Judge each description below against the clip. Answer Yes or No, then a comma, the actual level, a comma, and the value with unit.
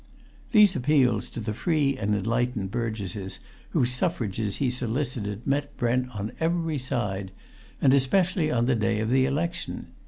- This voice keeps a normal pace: Yes, average, 150 wpm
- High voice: No, low, 125 Hz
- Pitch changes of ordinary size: Yes, average, 4.8 semitones